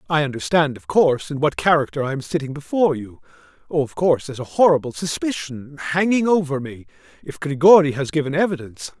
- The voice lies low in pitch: No, medium, 150 Hz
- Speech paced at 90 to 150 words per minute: No, average, 180 wpm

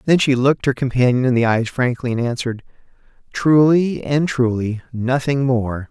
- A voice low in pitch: Yes, low, 125 Hz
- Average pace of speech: Yes, average, 165 wpm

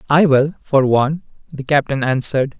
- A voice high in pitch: No, medium, 140 Hz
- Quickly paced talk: No, average, 160 wpm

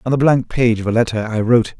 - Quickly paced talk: Yes, fast, 300 wpm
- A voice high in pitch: No, low, 115 Hz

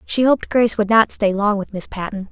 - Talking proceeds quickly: Yes, fast, 260 wpm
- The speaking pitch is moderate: No, high, 210 Hz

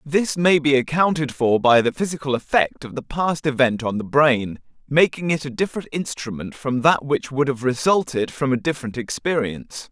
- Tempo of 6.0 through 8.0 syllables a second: No, 5.2 syllables/s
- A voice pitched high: No, medium, 140 Hz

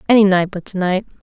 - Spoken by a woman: Yes, female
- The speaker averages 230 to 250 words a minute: Yes, fast, 235 wpm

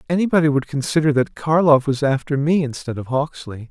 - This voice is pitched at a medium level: Yes, medium, 145 Hz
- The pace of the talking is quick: No, average, 180 wpm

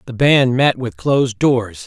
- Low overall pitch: Yes, low, 125 Hz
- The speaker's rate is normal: Yes, average, 195 wpm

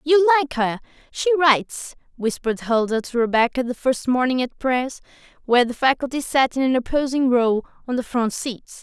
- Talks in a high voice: Yes, very high, 255 Hz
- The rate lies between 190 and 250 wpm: No, average, 175 wpm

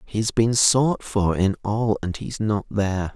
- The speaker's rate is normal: No, fast, 210 wpm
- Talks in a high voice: No, low, 105 Hz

